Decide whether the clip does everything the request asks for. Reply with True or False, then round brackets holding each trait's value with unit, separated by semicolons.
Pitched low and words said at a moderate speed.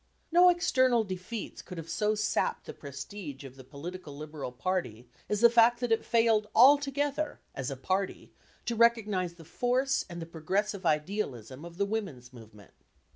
False (190 Hz; 165 wpm)